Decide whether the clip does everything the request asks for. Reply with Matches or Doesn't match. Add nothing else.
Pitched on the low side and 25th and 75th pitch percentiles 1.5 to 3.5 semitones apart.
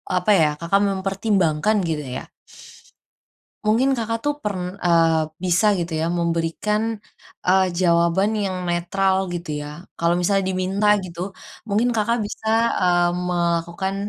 Doesn't match